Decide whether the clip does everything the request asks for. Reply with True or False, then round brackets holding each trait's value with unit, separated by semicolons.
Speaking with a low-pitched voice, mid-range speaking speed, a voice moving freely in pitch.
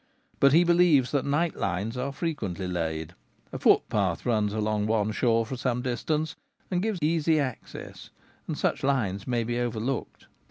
True (125 Hz; 160 wpm; 5.7 semitones)